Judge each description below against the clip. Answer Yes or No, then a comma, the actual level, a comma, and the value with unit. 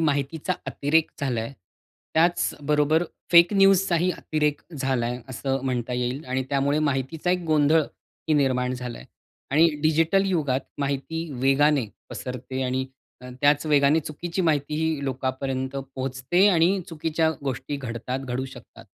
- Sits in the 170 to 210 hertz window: No, medium, 145 Hz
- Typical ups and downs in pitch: Yes, average, 3.6 semitones